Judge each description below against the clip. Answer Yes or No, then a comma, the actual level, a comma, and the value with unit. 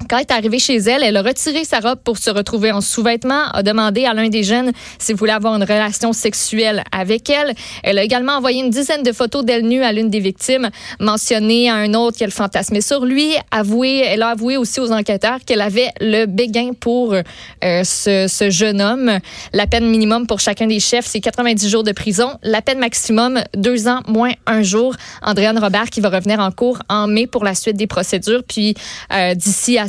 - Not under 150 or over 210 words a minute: No, fast, 220 wpm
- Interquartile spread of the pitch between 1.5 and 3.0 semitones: Yes, average, 2.7 semitones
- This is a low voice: No, high, 225 Hz